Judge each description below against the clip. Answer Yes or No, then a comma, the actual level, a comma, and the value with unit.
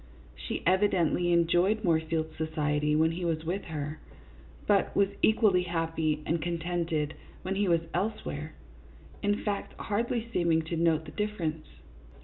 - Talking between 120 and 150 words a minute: Yes, slow, 135 wpm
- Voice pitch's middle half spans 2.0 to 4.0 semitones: Yes, average, 3.4 semitones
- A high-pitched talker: No, medium, 170 Hz